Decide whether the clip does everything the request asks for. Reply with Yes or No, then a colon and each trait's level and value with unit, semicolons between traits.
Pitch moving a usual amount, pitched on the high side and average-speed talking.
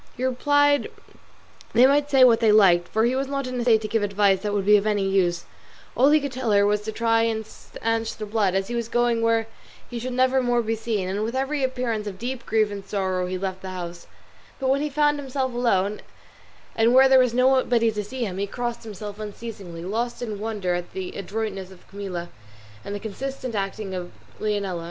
No: average, 4.0 semitones; high, 220 Hz; fast, 220 wpm